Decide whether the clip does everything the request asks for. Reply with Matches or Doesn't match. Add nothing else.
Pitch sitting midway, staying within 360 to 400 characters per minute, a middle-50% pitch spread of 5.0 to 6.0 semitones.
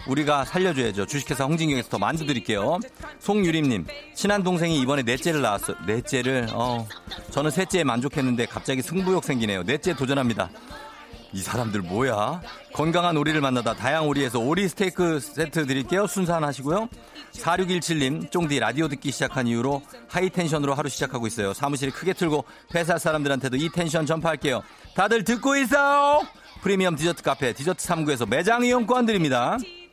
Matches